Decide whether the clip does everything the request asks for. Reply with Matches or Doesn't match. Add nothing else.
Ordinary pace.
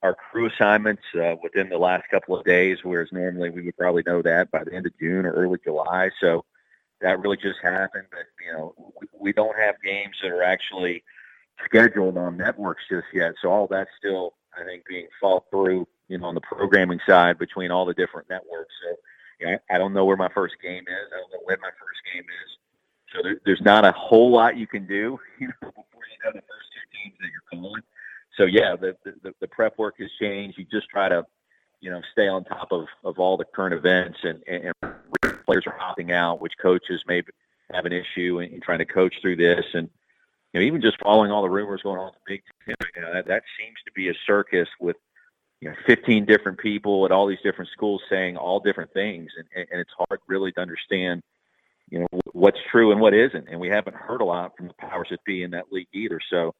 Doesn't match